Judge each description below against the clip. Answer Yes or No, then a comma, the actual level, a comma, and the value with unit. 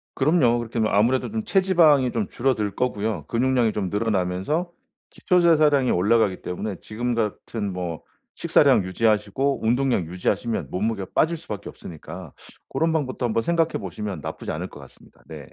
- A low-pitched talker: Yes, low, 115 Hz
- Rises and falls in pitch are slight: No, wide, 5.4 semitones